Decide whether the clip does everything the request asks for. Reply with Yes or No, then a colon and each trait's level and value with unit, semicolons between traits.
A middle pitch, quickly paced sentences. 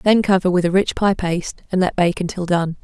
Yes: medium, 180 Hz; fast, 255 wpm